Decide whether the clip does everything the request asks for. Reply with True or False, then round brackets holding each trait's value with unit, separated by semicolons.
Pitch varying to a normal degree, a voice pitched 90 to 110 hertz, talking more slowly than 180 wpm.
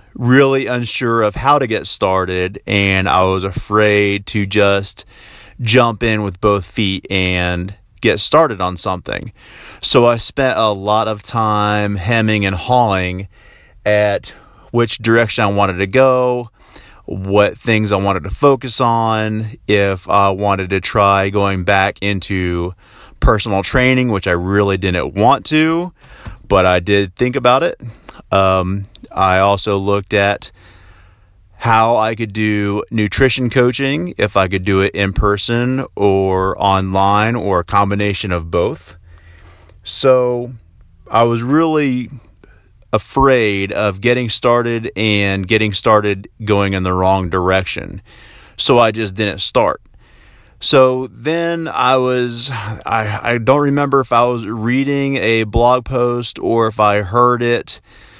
True (3.7 semitones; 105 Hz; 140 wpm)